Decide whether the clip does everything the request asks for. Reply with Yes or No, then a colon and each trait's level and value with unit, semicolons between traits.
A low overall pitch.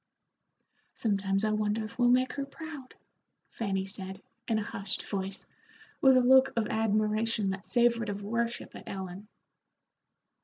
No: high, 215 Hz